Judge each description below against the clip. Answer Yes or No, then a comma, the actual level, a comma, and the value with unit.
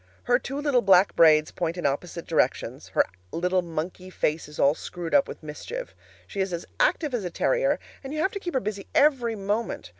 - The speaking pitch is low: No, high, 195 Hz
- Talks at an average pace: No, fast, 210 wpm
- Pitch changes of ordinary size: No, wide, 8.1 semitones